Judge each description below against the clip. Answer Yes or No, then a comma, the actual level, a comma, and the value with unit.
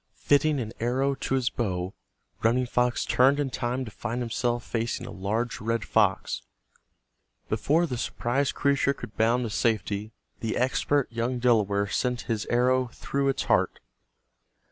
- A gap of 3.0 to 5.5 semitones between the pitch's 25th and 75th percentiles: No, narrow, 2.6 semitones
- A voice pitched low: Yes, low, 120 Hz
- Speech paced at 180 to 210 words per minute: No, average, 150 wpm